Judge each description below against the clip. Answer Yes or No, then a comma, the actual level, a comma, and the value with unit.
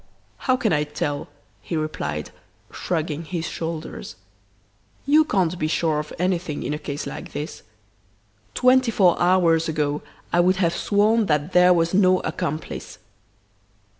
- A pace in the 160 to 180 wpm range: No, average, 140 wpm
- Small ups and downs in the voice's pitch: No, average, 3.4 semitones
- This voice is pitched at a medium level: Yes, medium, 170 Hz